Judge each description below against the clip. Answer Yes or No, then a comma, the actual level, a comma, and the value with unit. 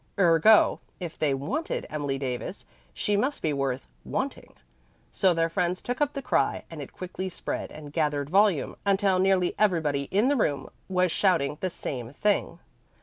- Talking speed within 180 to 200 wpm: No, average, 165 wpm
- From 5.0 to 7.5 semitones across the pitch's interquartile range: Yes, wide, 5.4 semitones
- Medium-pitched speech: Yes, medium, 175 Hz